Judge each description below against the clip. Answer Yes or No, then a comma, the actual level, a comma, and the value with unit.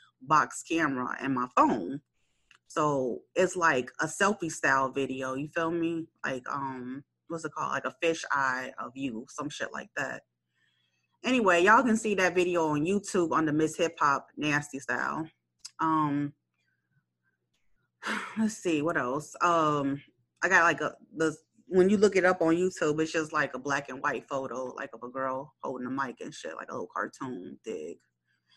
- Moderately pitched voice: Yes, medium, 150 Hz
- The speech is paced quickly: No, average, 180 wpm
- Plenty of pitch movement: No, average, 4.3 semitones